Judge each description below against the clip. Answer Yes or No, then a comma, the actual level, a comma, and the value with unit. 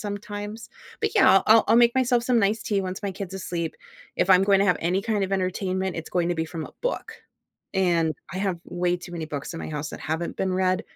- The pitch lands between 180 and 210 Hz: Yes, high, 190 Hz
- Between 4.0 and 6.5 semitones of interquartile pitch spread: No, average, 2.9 semitones